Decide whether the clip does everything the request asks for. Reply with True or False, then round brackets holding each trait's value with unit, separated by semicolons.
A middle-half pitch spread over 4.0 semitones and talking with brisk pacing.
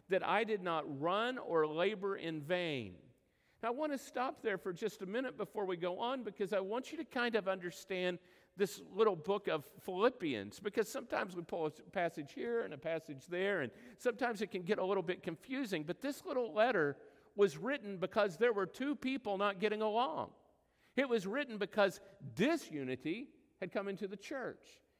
False (4.8 semitones; 190 wpm)